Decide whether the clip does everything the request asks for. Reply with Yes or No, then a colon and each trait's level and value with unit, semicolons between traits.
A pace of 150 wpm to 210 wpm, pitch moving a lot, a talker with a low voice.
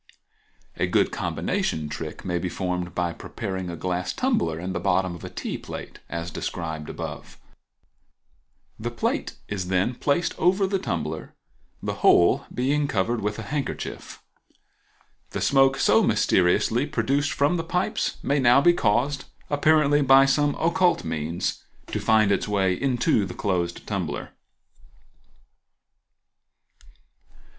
No: slow, 135 wpm; wide, 8.1 semitones; low, 110 Hz